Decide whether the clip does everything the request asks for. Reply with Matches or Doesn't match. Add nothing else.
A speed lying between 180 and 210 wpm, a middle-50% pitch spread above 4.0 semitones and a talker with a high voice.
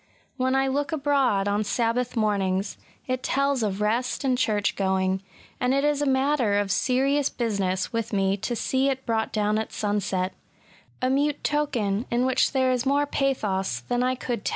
Matches